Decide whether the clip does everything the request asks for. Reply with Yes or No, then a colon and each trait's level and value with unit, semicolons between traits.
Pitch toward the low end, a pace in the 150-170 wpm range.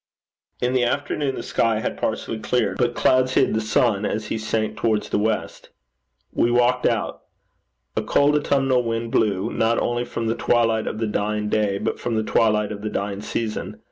No: low, 115 Hz; average, 190 wpm